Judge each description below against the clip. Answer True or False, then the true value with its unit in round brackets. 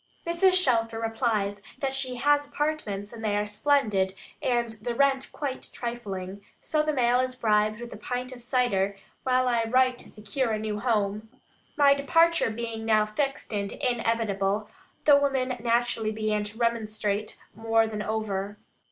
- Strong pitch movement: False (3.3 semitones)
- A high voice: True (230 Hz)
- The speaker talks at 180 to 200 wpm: False (160 wpm)